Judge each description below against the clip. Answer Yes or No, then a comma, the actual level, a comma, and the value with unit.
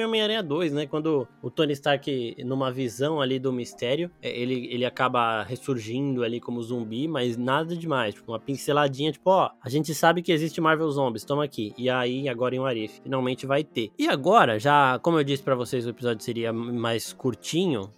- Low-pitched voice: Yes, low, 130 Hz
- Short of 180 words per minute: No, fast, 185 wpm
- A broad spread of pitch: No, average, 3.6 semitones